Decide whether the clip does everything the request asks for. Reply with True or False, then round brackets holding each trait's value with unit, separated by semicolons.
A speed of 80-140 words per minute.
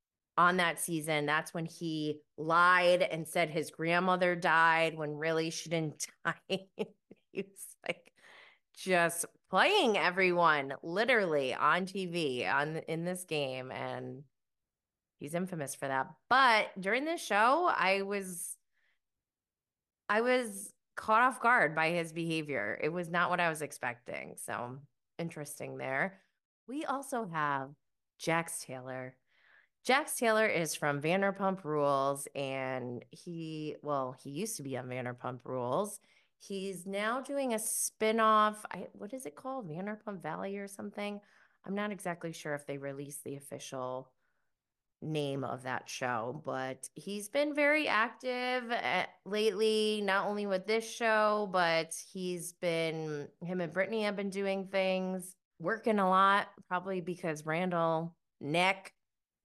True (135 wpm)